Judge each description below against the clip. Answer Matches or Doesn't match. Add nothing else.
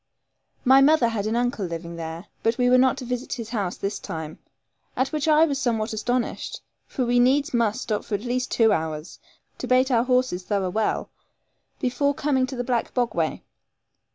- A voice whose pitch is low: Doesn't match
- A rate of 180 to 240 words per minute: Matches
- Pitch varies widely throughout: Doesn't match